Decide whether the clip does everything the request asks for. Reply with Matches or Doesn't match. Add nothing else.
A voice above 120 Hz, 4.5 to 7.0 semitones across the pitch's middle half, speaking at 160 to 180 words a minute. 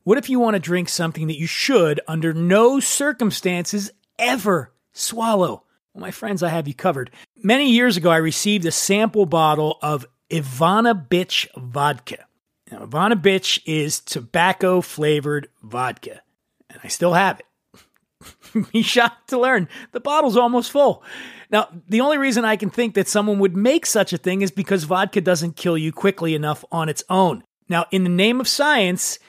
Matches